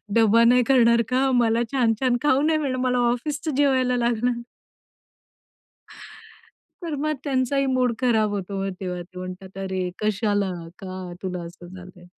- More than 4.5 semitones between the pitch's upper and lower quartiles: Yes, average, 5.2 semitones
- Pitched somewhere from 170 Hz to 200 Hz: No, high, 235 Hz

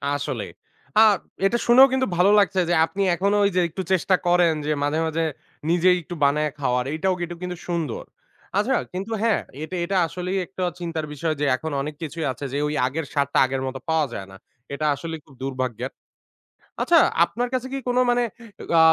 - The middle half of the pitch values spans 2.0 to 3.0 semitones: No, average, 4.5 semitones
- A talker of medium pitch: Yes, medium, 165 Hz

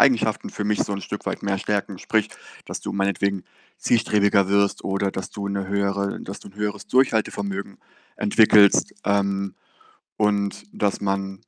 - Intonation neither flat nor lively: No, narrow, 0.9 semitones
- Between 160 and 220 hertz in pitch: No, low, 100 Hz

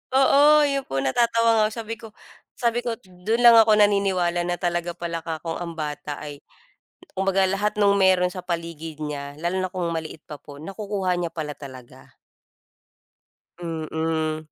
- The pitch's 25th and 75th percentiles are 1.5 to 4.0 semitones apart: No, average, 4.5 semitones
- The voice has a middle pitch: Yes, medium, 175 Hz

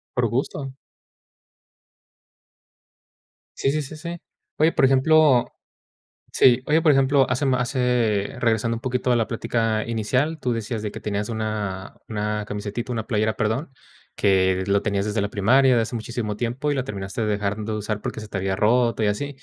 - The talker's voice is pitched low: Yes, low, 115 Hz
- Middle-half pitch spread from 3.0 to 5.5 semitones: Yes, average, 3.7 semitones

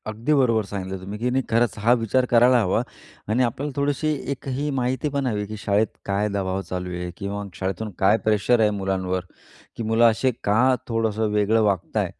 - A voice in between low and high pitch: No, low, 110 Hz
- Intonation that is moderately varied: Yes, average, 3.7 semitones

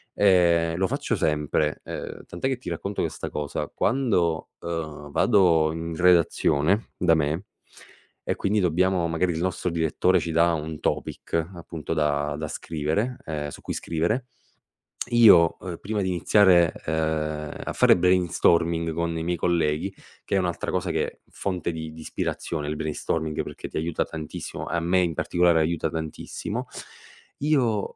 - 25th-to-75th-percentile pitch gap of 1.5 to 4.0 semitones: Yes, average, 2.7 semitones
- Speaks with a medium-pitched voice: No, very low, 85 Hz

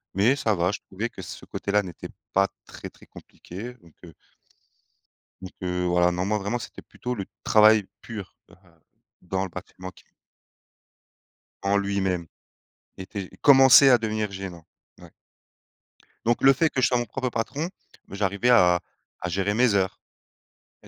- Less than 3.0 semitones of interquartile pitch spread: No, average, 4.2 semitones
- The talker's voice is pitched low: Yes, low, 100 Hz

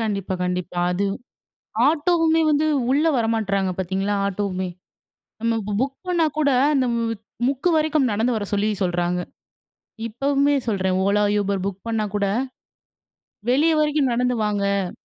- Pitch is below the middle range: No, high, 220 Hz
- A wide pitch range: Yes, wide, 6.0 semitones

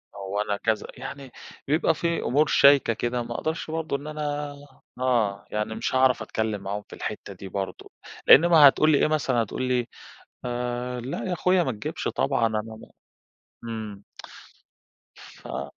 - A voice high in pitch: No, low, 125 Hz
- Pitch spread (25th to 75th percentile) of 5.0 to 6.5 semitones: Yes, wide, 5.4 semitones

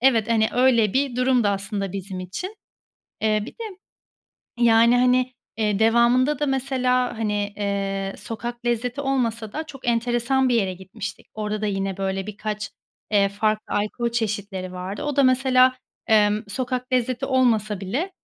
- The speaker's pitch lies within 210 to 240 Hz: Yes, high, 225 Hz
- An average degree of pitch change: Yes, average, 3.7 semitones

